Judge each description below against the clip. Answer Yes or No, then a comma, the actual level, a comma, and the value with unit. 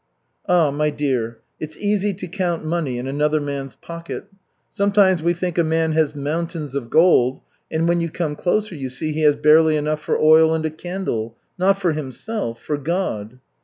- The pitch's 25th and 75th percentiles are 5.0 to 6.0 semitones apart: No, average, 3.2 semitones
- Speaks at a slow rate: No, average, 185 wpm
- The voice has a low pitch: No, medium, 155 Hz